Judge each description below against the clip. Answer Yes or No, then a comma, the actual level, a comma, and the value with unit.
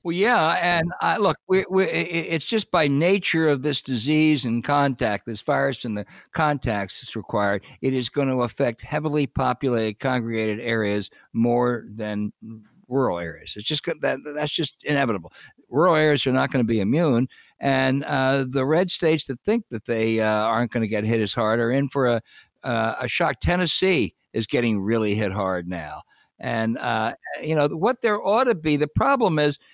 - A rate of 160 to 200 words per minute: Yes, average, 190 wpm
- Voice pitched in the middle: No, low, 130 Hz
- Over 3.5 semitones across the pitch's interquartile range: Yes, wide, 5.4 semitones